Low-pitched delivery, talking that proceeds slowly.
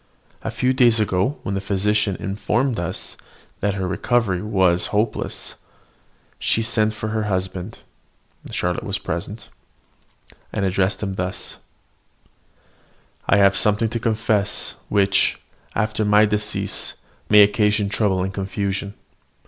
Yes: low, 105 Hz; slow, 125 wpm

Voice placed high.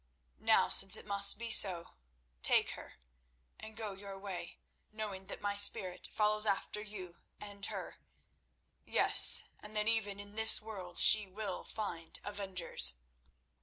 Yes: high, 205 Hz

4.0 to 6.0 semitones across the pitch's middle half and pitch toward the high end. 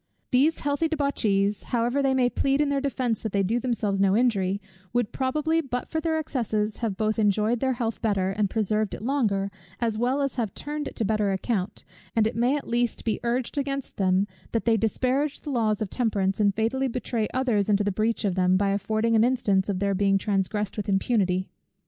Yes: average, 4.3 semitones; high, 225 Hz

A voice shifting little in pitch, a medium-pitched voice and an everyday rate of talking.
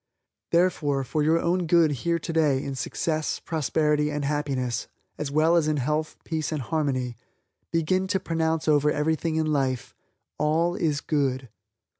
Yes: narrow, 2.3 semitones; medium, 155 Hz; average, 150 wpm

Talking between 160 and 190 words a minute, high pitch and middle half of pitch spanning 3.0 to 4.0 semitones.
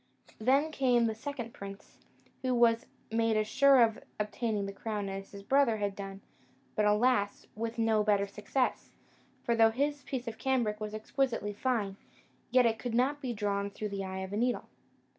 Yes: average, 180 wpm; high, 225 Hz; average, 3.5 semitones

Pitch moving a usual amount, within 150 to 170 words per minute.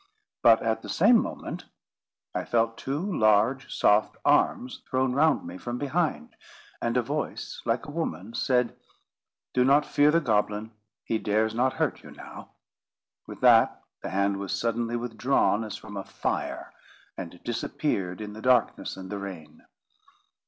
Yes: average, 4.1 semitones; average, 155 wpm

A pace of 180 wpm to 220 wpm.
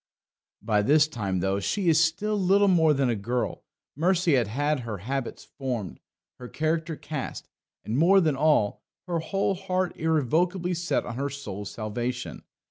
No: average, 155 wpm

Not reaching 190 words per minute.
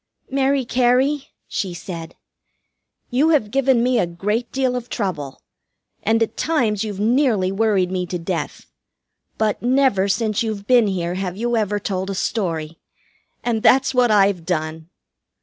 Yes: average, 150 wpm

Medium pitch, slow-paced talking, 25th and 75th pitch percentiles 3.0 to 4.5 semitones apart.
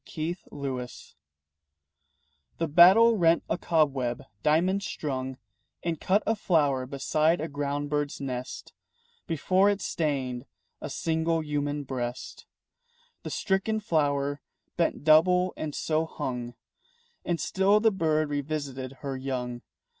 Yes: medium, 150 Hz; slow, 120 wpm; average, 3.8 semitones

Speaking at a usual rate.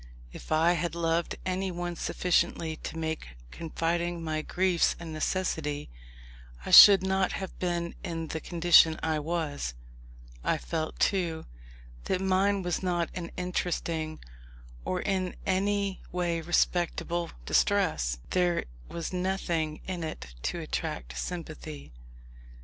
No: slow, 120 wpm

